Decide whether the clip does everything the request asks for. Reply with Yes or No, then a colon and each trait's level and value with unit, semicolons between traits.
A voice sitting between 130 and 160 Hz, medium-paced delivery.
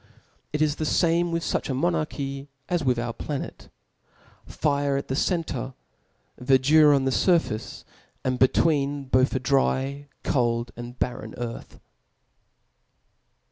No: medium, 140 Hz; slow, 130 wpm